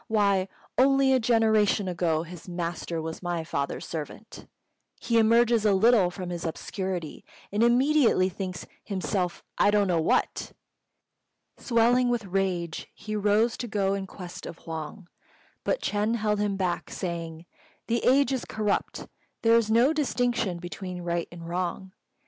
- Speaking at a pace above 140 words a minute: Yes, average, 150 wpm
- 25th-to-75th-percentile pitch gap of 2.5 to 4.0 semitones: No, average, 4.6 semitones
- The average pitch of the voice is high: Yes, high, 195 Hz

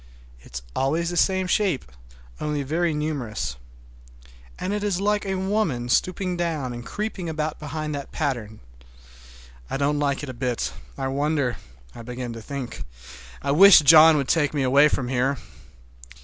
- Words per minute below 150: No, average, 155 wpm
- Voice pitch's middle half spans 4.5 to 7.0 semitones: Yes, average, 5.2 semitones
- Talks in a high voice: No, medium, 145 Hz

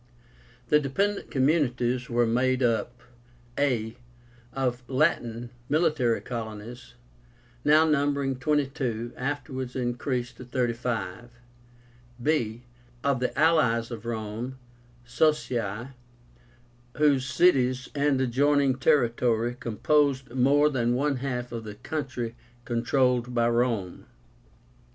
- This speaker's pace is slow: Yes, slow, 105 wpm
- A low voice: Yes, low, 125 Hz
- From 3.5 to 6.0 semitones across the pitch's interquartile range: No, average, 3.0 semitones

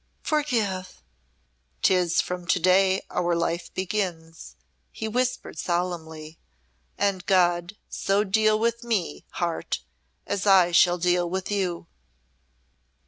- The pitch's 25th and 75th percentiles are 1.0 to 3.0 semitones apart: Yes, average, 2.7 semitones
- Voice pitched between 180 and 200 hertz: Yes, medium, 185 Hz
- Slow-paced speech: Yes, slow, 110 wpm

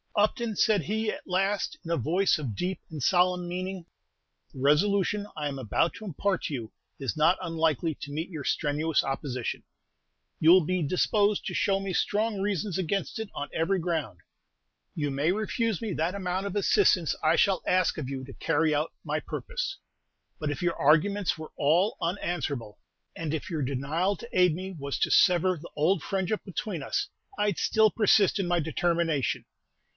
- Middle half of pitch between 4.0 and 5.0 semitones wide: Yes, average, 4.5 semitones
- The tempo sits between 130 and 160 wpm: No, average, 180 wpm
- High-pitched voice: No, medium, 175 Hz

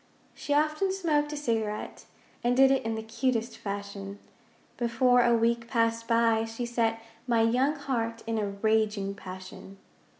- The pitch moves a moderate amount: No, narrow, 2.3 semitones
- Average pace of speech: Yes, average, 155 wpm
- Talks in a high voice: Yes, high, 230 Hz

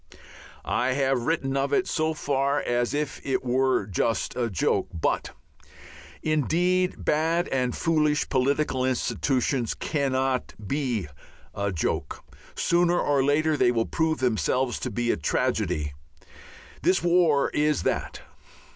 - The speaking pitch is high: No, low, 135 Hz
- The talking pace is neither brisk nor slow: No, slow, 120 wpm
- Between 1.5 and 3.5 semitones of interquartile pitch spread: No, average, 3.9 semitones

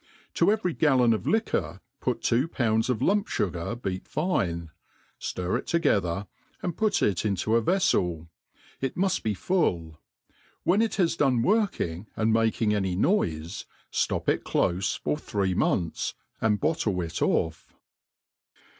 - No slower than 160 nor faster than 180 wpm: No, average, 140 wpm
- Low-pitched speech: Yes, low, 110 Hz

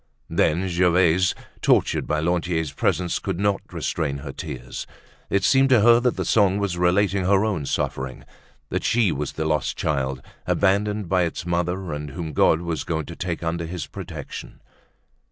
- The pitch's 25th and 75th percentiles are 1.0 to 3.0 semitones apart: No, average, 3.6 semitones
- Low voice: Yes, very low, 85 Hz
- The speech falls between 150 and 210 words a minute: Yes, average, 170 wpm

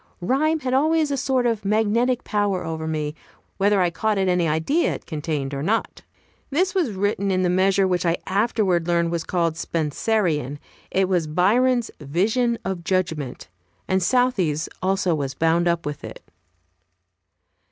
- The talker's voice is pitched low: No, medium, 185 Hz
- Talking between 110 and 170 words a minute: Yes, average, 160 wpm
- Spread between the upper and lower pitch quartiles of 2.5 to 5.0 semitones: No, wide, 5.4 semitones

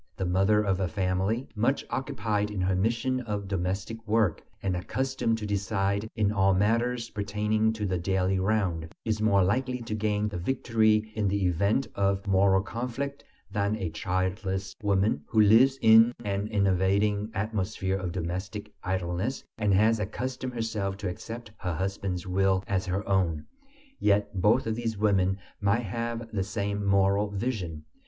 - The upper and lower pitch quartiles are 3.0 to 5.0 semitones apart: No, narrow, 2.6 semitones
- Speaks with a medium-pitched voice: No, low, 100 Hz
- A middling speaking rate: Yes, average, 160 wpm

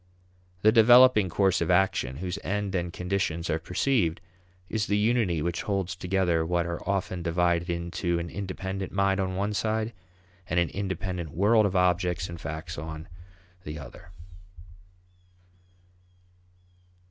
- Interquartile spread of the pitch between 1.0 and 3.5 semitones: Yes, narrow, 2.6 semitones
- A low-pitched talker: Yes, very low, 90 Hz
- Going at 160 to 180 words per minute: No, slow, 135 wpm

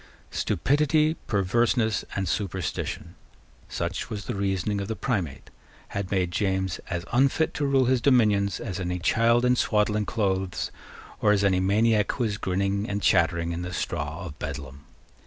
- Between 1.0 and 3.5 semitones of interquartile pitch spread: No, average, 4.0 semitones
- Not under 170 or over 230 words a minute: No, average, 155 wpm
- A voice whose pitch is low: Yes, low, 100 Hz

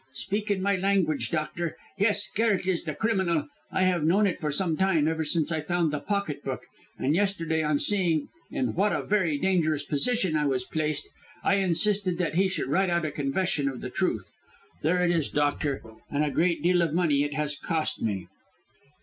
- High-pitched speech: No, medium, 165 Hz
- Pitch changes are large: No, average, 4.1 semitones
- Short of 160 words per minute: No, average, 200 wpm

